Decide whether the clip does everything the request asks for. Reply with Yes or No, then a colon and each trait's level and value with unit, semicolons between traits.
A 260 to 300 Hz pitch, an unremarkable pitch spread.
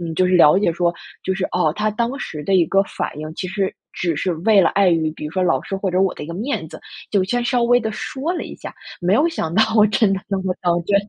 No: high, 190 Hz; average, 3.8 semitones